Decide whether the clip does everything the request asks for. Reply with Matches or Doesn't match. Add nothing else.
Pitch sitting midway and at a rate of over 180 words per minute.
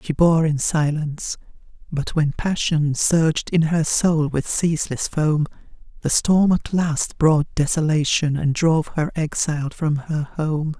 Doesn't match